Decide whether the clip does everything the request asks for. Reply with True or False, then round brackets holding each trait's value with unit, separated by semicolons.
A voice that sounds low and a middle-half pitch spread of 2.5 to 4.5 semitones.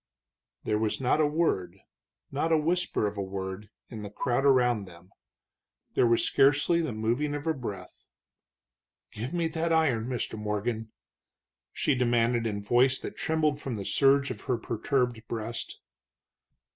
False (120 Hz; 5.2 semitones)